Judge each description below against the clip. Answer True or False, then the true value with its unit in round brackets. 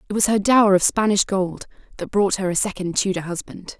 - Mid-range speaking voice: False (195 Hz)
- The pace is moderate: False (220 wpm)